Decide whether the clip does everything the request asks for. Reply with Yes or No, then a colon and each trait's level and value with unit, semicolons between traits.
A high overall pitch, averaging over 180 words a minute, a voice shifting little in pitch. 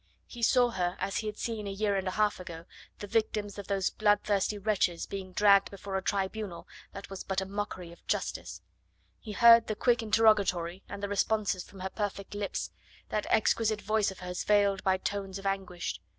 Yes: high, 200 Hz; average, 195 wpm; narrow, 1.9 semitones